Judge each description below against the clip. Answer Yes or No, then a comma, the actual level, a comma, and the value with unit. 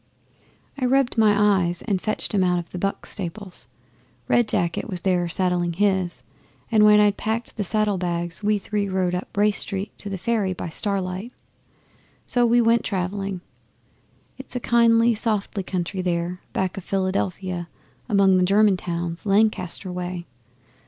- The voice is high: Yes, high, 195 Hz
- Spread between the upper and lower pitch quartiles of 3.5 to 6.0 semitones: No, average, 2.9 semitones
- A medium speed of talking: Yes, average, 160 wpm